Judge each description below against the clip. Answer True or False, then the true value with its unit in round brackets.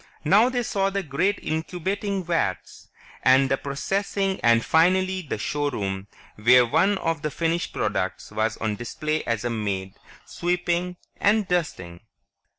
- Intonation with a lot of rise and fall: True (8.1 semitones)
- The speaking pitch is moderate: True (160 Hz)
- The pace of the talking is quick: False (140 wpm)